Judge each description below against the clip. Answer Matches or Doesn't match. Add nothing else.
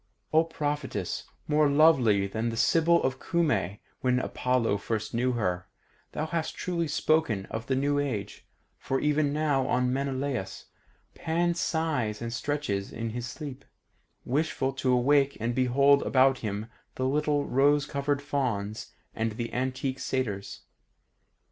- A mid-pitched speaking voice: Doesn't match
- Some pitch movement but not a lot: Matches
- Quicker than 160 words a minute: Doesn't match